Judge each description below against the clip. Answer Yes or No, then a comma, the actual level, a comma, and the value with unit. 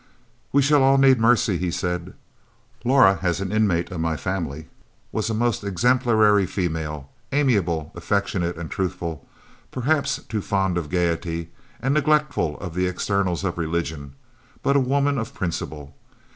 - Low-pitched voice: Yes, very low, 95 Hz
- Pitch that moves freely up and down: Yes, wide, 6.2 semitones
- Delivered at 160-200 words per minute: No, average, 145 wpm